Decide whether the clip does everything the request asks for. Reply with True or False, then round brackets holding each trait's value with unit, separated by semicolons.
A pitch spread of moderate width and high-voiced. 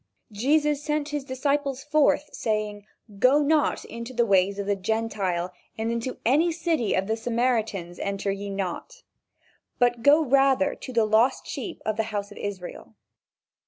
False (5.8 semitones; 235 Hz)